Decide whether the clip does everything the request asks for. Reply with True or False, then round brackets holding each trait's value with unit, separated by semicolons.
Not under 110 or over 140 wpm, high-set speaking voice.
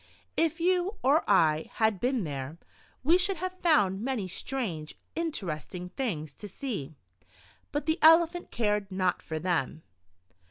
True (135 wpm; 220 Hz)